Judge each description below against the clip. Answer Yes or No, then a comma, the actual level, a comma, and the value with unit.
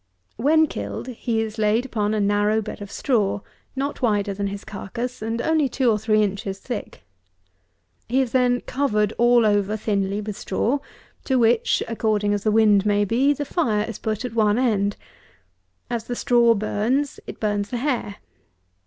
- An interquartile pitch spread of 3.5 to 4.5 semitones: No, average, 3.0 semitones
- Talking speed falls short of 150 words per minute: No, average, 175 wpm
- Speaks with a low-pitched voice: No, high, 220 Hz